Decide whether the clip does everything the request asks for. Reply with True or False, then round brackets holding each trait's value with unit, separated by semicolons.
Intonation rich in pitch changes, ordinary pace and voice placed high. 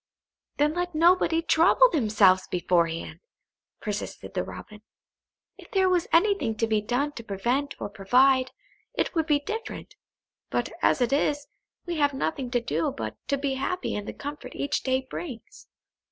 True (6.7 semitones; 160 wpm; 275 Hz)